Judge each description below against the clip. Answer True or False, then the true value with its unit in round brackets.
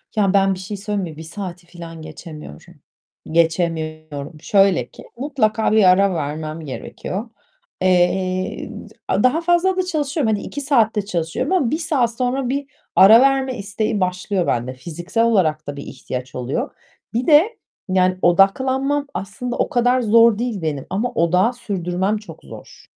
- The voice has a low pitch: False (195 Hz)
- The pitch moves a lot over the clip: True (6.5 semitones)